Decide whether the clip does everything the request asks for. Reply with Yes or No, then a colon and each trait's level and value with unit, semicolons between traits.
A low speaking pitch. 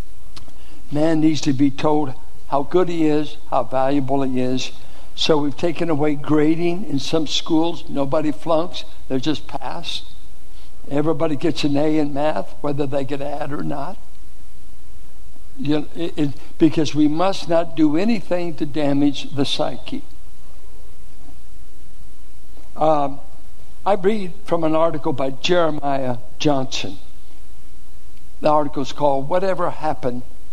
No: medium, 150 Hz